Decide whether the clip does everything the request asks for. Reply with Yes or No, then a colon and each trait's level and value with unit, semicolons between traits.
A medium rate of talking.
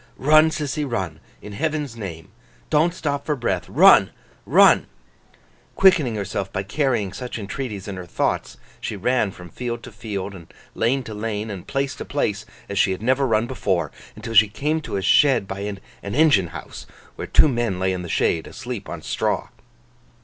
Yes: average, 180 wpm